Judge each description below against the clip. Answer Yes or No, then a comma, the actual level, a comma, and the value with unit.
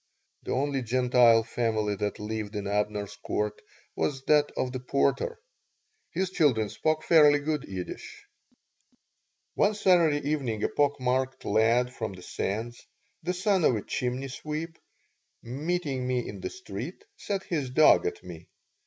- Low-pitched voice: Yes, low, 130 Hz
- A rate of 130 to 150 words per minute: Yes, average, 145 wpm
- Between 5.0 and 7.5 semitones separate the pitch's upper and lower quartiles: Yes, wide, 5.6 semitones